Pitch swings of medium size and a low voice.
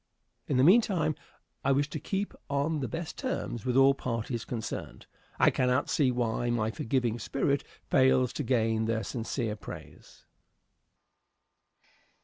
Yes: average, 3.5 semitones; low, 130 Hz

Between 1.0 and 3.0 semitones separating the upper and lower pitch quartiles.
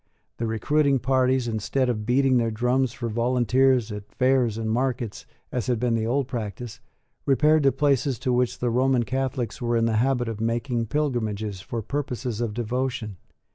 Yes: narrow, 2.6 semitones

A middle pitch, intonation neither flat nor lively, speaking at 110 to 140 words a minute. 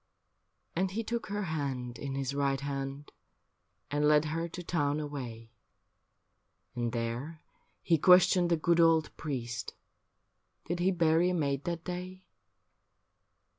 Yes: medium, 155 Hz; average, 4.0 semitones; slow, 135 wpm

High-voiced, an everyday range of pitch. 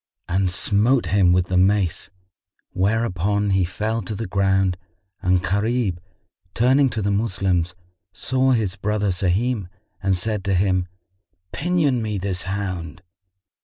No: low, 100 Hz; average, 3.3 semitones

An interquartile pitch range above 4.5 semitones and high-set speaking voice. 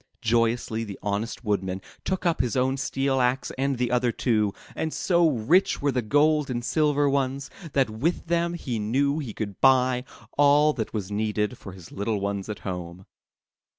No: average, 4.9 semitones; low, 125 Hz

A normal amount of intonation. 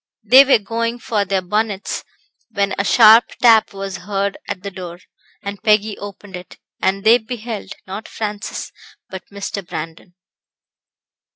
No: narrow, 2.3 semitones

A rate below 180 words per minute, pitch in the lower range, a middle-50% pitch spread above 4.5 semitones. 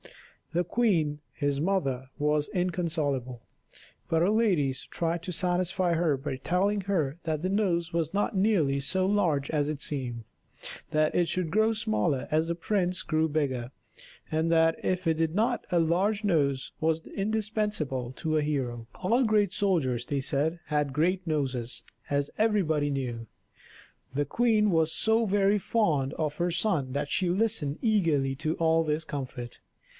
No: average, 160 wpm; medium, 160 Hz; average, 4.9 semitones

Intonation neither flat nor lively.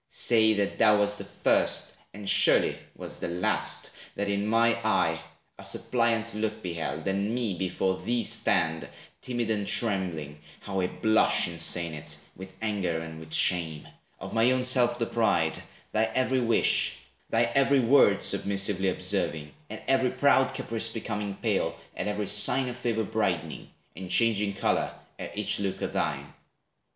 Yes: average, 3.7 semitones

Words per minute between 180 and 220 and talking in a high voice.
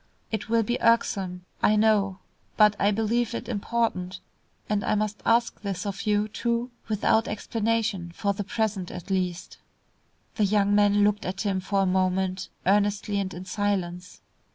No: average, 160 wpm; high, 205 Hz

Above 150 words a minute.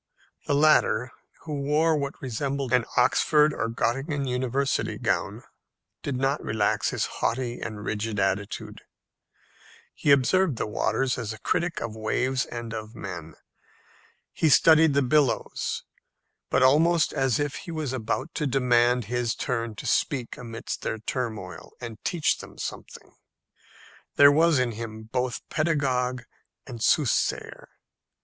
No: slow, 135 wpm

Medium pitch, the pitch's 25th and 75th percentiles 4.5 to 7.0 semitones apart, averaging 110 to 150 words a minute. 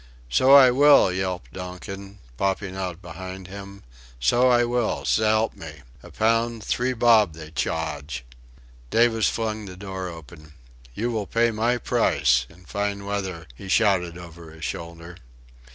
No: very low, 95 Hz; average, 4.8 semitones; average, 145 wpm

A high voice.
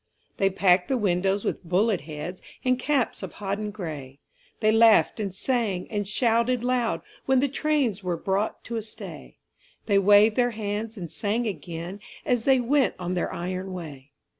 Yes: high, 205 Hz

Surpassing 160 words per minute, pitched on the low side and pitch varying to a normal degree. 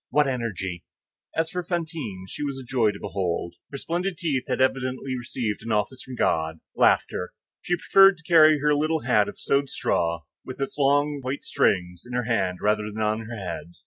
No: average, 190 wpm; low, 130 Hz; wide, 6.2 semitones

